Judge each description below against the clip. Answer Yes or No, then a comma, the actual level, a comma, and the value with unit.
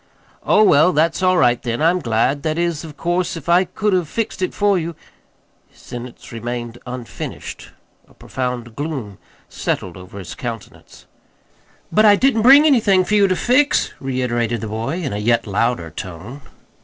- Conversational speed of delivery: Yes, average, 170 wpm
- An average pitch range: No, wide, 7.6 semitones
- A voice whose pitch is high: No, medium, 145 Hz